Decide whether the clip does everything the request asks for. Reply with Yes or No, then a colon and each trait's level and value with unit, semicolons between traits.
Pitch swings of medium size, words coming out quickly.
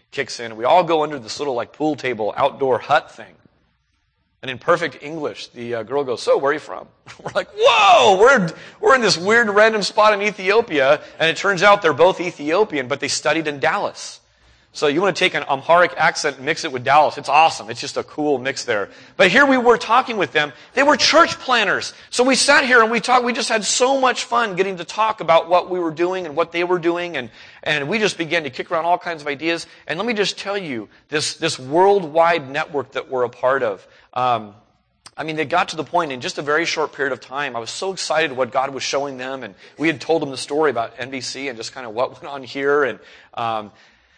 No: wide, 6.1 semitones; fast, 245 wpm